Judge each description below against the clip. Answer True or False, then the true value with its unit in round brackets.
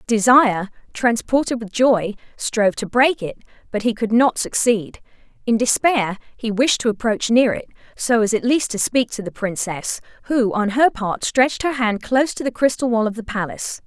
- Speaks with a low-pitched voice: False (230 Hz)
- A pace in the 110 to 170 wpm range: False (195 wpm)